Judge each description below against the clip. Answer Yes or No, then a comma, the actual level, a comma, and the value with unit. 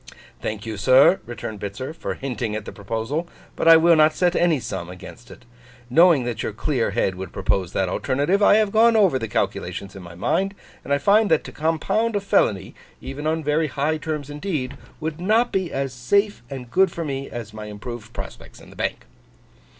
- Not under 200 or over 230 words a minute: Yes, fast, 205 wpm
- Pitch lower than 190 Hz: Yes, medium, 140 Hz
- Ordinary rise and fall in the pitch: No, wide, 7.1 semitones